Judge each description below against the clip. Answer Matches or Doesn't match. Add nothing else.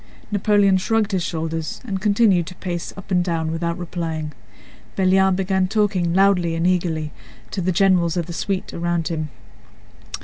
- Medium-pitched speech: Matches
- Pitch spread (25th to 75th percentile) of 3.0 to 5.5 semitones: Doesn't match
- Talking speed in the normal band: Matches